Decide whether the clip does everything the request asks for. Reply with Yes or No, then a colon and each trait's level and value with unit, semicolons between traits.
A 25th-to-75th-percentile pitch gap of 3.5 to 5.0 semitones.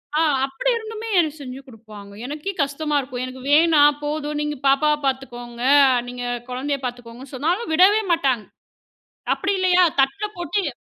Yes: average, 4.1 semitones